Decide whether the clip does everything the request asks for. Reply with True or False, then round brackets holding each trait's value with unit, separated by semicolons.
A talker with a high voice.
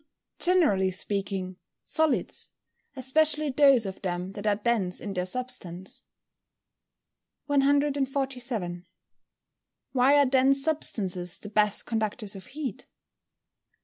True (235 Hz)